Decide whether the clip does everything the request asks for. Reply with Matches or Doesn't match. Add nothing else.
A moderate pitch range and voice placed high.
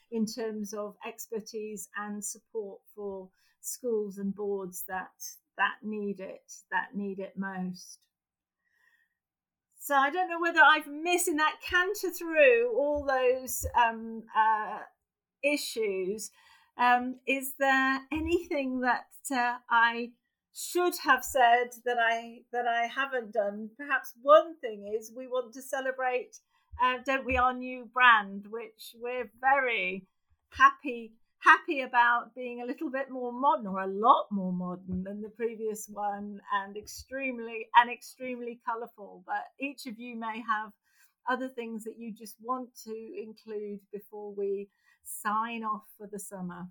Matches